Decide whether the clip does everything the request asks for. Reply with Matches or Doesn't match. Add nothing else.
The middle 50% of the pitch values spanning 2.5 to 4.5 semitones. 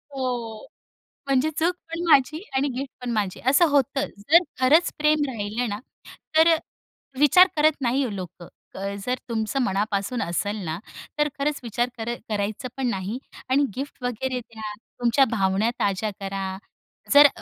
Doesn't match